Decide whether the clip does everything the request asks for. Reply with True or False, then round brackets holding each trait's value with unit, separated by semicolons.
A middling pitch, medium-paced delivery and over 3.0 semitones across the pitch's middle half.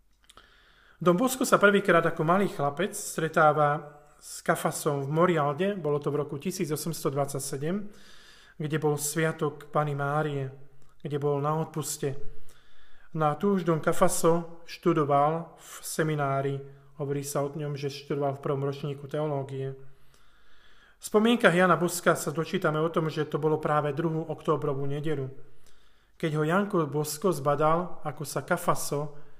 False (155 Hz; 140 wpm; 2.7 semitones)